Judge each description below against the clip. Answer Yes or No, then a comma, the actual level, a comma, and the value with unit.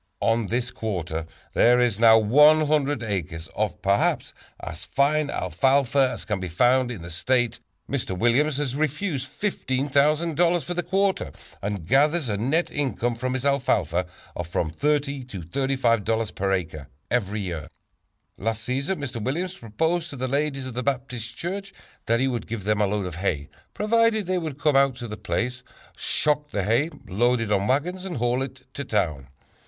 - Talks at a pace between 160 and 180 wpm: Yes, average, 175 wpm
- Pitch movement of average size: No, wide, 5.8 semitones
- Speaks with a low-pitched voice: Yes, low, 125 Hz